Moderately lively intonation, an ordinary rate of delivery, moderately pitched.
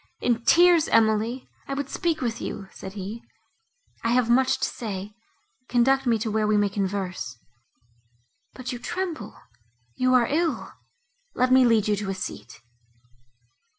No: average, 4.1 semitones; average, 150 wpm; high, 230 Hz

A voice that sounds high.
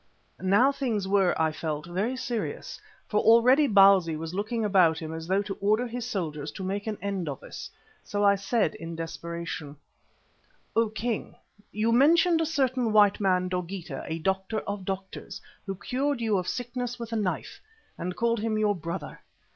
Yes: high, 200 Hz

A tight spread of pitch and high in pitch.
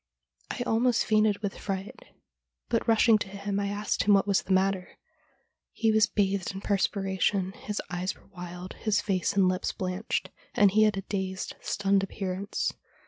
Yes: narrow, 1.7 semitones; high, 200 Hz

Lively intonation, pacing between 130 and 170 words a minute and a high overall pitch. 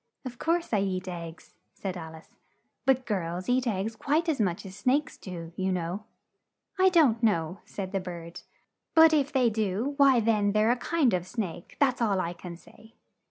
No: wide, 5.9 semitones; average, 190 wpm; high, 210 Hz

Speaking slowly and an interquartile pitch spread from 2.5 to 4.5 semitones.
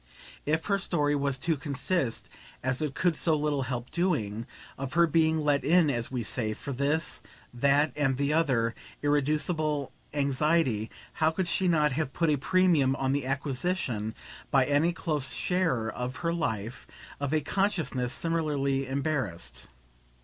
No: average, 155 wpm; average, 3.6 semitones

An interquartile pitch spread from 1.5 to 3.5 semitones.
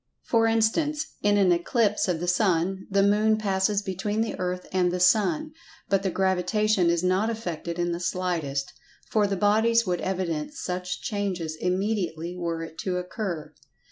Yes: average, 3.0 semitones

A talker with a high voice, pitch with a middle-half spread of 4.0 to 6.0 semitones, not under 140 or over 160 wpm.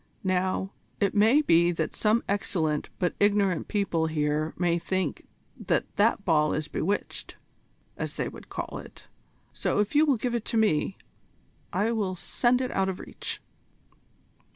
Yes: high, 195 Hz; average, 4.3 semitones; average, 155 wpm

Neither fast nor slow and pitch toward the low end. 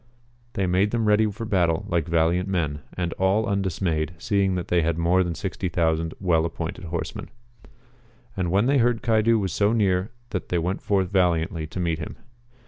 Yes: average, 175 wpm; very low, 90 Hz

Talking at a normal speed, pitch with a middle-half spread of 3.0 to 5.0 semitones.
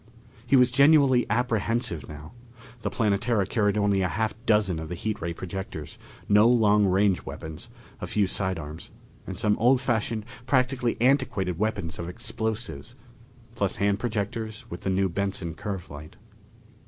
Yes: average, 155 wpm; average, 4.0 semitones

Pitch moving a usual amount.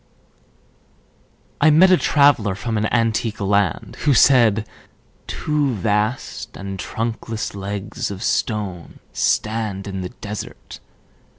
Yes: average, 3.1 semitones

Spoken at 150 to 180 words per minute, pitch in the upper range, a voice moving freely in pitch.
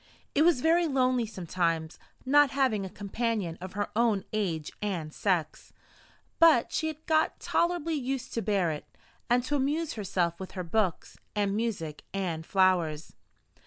Yes: average, 155 wpm; high, 210 Hz; wide, 7.0 semitones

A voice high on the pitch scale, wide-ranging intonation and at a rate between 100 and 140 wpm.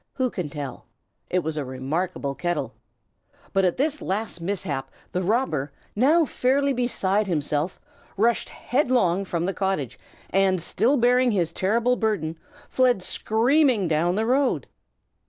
Yes: high, 195 Hz; wide, 6.7 semitones; slow, 135 wpm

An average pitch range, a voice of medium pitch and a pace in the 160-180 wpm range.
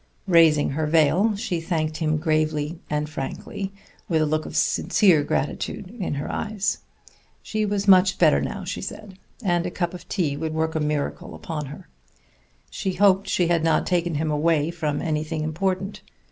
Yes: average, 3.3 semitones; medium, 165 Hz; average, 175 wpm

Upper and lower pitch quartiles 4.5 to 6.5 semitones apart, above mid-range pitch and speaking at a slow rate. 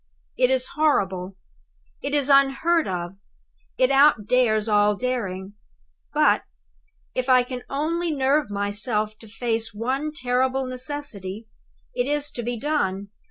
Yes: average, 5.1 semitones; very high, 250 Hz; slow, 125 wpm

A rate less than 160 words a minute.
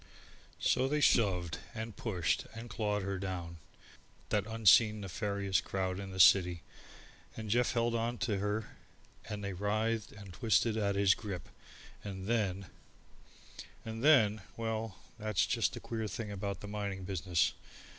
Yes: average, 145 wpm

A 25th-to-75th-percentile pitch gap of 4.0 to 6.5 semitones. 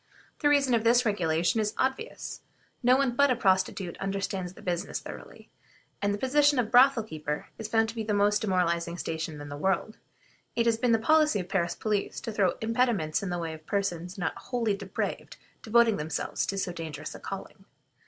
Yes: average, 5.1 semitones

